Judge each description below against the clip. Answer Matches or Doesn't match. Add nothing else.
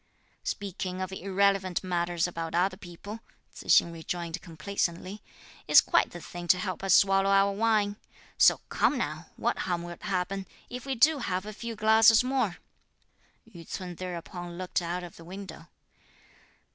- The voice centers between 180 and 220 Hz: Matches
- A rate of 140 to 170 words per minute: Matches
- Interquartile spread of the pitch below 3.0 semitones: Matches